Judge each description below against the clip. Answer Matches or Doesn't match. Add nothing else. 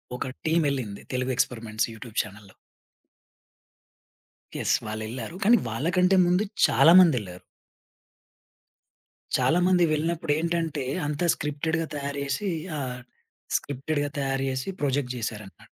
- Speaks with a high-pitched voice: Doesn't match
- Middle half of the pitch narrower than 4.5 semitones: Doesn't match